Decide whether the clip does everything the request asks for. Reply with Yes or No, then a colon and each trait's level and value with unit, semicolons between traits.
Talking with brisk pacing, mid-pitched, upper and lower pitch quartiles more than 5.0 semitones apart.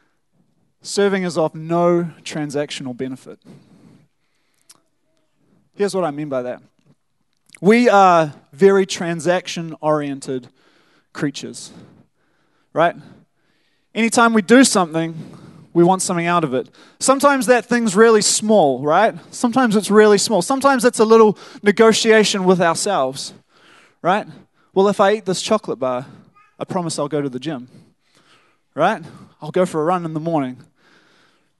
No: slow, 135 wpm; medium, 180 Hz; wide, 5.4 semitones